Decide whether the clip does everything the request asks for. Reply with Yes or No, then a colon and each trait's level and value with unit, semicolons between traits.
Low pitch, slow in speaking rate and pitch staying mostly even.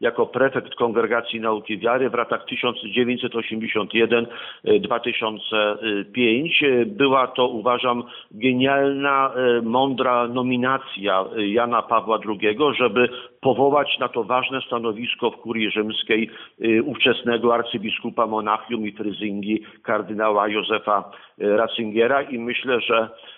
Yes: low, 115 Hz; slow, 100 wpm; narrow, 2.3 semitones